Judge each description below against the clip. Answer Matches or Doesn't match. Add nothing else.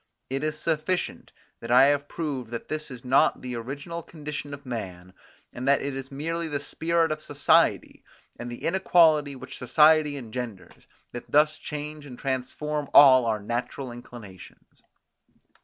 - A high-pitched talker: Doesn't match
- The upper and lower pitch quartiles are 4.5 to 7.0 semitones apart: Doesn't match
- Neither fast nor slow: Matches